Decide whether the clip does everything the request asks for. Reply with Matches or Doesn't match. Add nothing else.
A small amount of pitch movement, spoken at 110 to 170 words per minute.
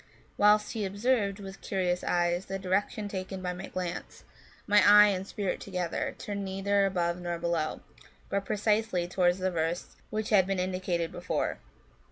Matches